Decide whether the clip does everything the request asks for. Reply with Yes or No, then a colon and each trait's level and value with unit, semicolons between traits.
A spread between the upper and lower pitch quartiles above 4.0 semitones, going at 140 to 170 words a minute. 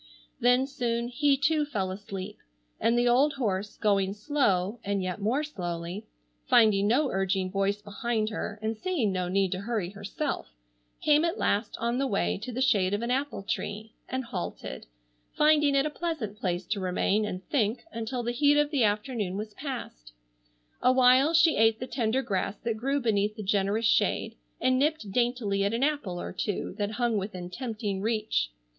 No: average, 4.6 semitones; average, 180 wpm